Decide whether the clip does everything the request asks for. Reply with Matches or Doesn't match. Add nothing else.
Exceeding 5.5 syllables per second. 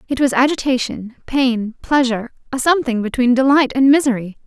Matches